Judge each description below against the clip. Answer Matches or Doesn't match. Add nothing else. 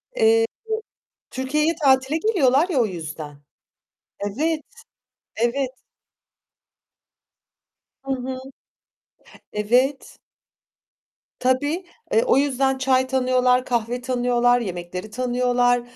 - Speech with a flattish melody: Matches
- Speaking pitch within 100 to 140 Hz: Doesn't match